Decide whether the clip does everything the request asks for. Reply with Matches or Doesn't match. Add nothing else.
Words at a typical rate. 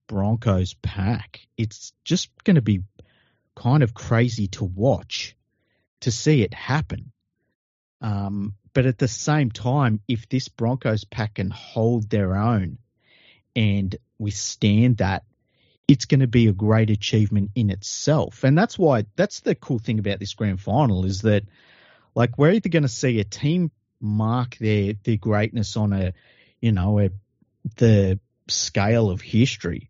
Matches